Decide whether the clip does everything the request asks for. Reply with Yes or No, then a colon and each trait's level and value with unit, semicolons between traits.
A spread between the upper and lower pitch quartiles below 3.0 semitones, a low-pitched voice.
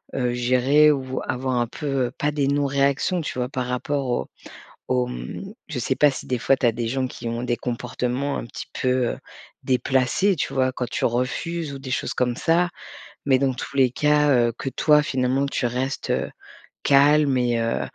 Yes: narrow, 2.4 semitones; low, 130 Hz